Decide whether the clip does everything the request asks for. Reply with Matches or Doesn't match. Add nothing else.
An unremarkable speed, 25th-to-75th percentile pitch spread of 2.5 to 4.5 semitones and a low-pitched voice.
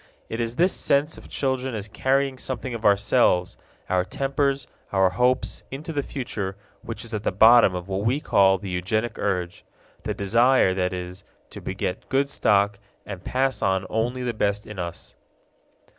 Doesn't match